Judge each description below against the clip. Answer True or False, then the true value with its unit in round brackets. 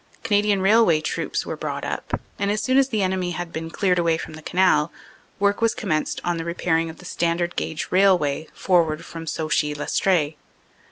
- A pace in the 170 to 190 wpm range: True (185 wpm)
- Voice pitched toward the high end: False (175 Hz)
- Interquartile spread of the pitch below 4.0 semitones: True (3.4 semitones)